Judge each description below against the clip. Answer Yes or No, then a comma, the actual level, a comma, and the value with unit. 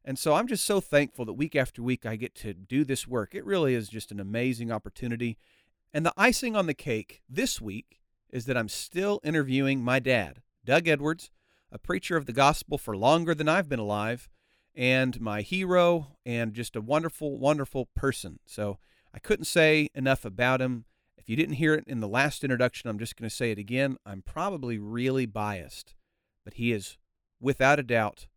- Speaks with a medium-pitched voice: No, low, 125 Hz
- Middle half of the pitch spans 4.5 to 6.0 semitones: Yes, average, 5.0 semitones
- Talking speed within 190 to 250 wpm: Yes, average, 195 wpm